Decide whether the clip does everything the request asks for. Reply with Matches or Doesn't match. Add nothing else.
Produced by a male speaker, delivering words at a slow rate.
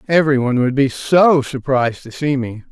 Doesn't match